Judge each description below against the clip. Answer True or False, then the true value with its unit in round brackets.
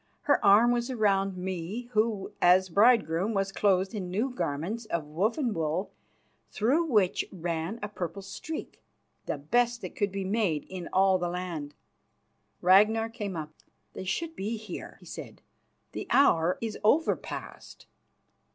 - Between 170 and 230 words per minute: False (150 wpm)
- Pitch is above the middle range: True (195 Hz)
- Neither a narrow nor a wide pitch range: True (4.1 semitones)